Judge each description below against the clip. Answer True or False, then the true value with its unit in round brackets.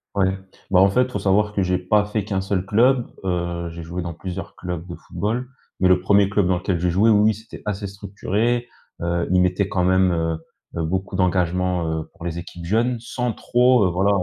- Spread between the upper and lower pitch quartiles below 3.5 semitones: True (2.8 semitones)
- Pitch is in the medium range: False (95 Hz)